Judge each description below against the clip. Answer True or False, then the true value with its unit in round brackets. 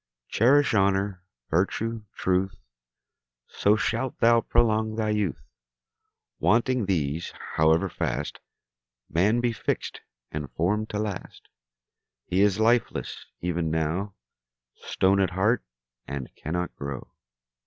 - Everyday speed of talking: False (110 wpm)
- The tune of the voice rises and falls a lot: False (4.1 semitones)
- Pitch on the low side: True (100 Hz)